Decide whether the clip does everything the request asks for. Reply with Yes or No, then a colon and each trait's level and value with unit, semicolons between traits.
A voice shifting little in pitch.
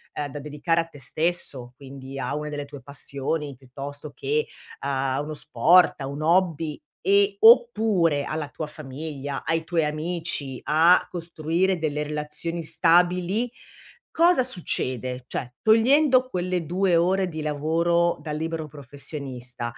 No: average, 3.7 semitones